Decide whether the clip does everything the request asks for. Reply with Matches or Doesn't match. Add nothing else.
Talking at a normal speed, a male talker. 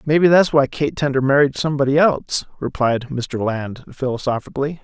Matches